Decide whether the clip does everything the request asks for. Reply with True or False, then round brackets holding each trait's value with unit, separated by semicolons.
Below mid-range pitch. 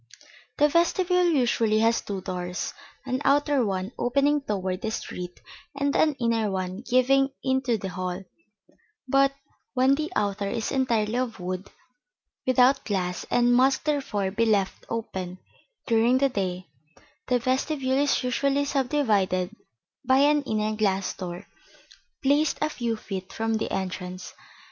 False (230 Hz)